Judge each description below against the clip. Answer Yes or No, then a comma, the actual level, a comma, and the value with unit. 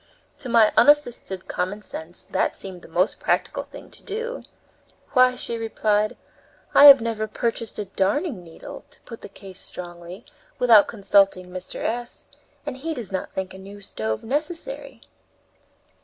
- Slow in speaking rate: No, average, 155 wpm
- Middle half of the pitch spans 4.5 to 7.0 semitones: Yes, average, 4.9 semitones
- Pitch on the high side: Yes, high, 215 Hz